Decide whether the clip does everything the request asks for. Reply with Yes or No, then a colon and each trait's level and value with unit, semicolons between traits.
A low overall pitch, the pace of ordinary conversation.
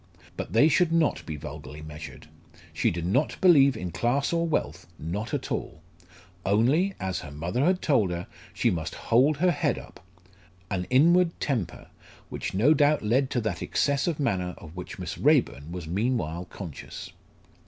Yes: low, 115 Hz; average, 170 wpm